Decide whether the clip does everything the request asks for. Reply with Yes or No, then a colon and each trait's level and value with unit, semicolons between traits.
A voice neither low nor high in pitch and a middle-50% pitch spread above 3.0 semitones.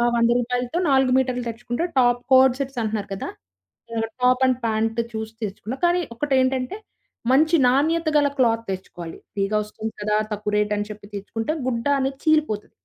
No: high, 240 Hz; average, 3.8 semitones